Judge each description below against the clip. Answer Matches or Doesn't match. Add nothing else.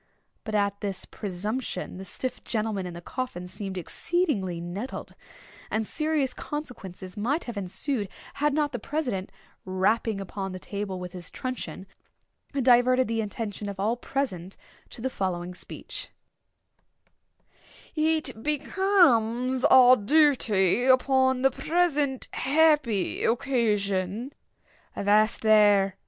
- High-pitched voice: Matches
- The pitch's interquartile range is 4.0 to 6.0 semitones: Matches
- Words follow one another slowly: Matches